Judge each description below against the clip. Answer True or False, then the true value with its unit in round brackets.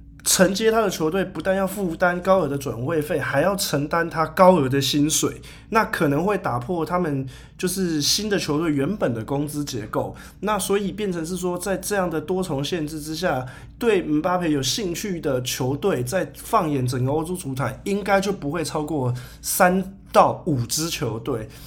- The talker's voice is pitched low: False (155 Hz)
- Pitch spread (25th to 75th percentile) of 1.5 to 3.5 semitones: False (4.7 semitones)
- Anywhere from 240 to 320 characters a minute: True (270 characters per minute)